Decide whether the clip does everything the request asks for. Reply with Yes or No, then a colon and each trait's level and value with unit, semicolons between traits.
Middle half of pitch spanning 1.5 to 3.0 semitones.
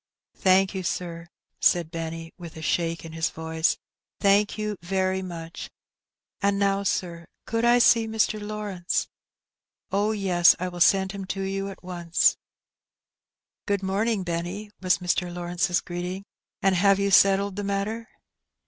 Yes: narrow, 2.4 semitones